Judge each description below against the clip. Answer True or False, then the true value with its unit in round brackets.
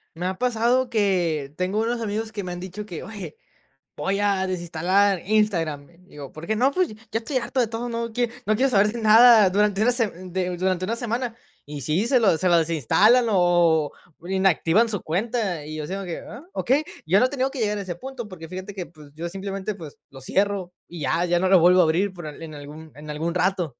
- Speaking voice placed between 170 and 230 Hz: True (190 Hz)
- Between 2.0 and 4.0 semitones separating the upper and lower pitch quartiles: False (4.6 semitones)